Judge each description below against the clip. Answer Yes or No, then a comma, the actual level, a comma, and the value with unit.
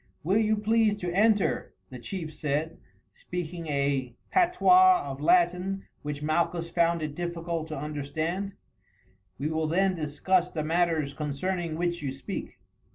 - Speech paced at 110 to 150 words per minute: Yes, average, 140 wpm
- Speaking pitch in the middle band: Yes, medium, 170 Hz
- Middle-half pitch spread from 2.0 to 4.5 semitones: Yes, average, 3.7 semitones